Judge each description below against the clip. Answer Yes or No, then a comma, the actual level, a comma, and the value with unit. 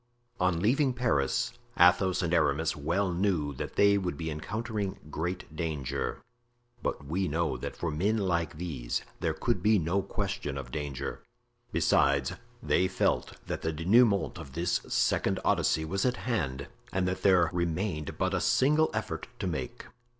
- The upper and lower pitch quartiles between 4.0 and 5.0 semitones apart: Yes, average, 4.5 semitones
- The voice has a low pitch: Yes, very low, 85 Hz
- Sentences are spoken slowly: No, average, 155 wpm